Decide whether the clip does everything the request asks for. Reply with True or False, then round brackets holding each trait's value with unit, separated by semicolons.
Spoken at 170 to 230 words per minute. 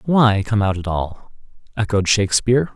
False (155 wpm)